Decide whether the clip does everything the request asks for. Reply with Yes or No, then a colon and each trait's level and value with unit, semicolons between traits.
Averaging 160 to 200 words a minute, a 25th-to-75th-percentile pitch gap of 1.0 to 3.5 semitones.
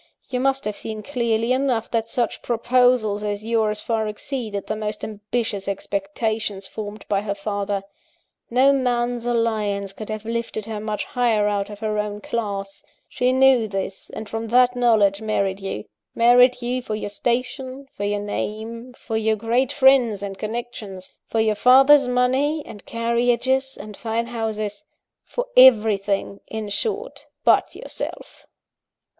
No: average, 150 wpm; average, 3.0 semitones